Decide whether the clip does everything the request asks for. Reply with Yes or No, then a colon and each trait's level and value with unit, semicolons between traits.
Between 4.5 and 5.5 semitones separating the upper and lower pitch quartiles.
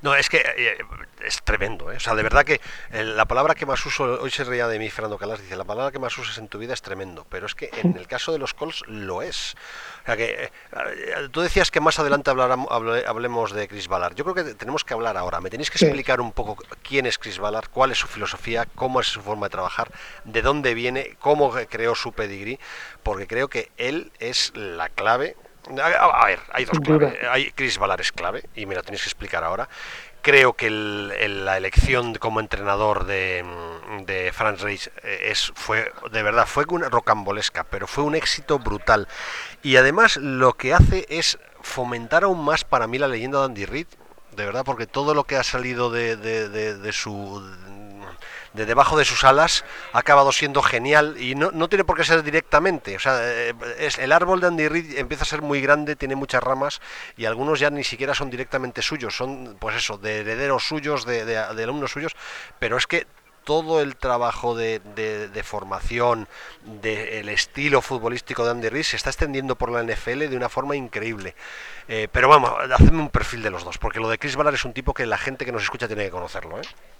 Yes: average, 5.0 semitones